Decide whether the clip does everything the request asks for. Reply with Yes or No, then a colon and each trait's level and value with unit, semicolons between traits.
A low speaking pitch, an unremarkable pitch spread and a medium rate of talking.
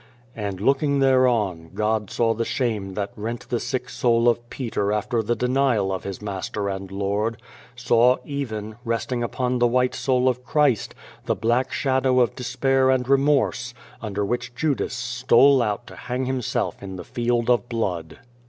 Yes: low, 120 Hz; average, 3.3 semitones; average, 170 wpm